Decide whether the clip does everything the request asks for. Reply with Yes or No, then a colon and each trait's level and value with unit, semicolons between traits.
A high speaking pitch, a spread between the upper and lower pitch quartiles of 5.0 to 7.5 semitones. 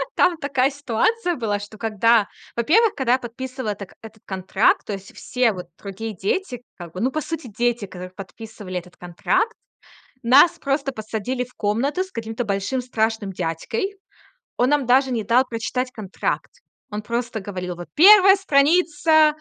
Yes: high, 235 Hz; average, 5.3 semitones